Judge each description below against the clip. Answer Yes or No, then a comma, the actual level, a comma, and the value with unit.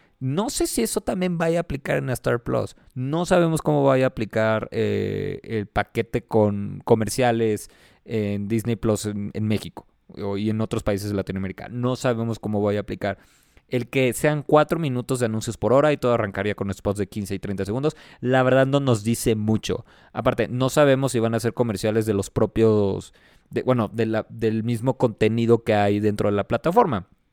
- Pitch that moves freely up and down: No, average, 3.8 semitones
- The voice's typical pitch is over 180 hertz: No, low, 115 Hz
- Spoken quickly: Yes, fast, 195 wpm